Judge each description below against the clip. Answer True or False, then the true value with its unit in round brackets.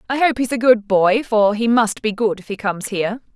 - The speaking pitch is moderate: False (220 Hz)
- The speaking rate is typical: False (270 wpm)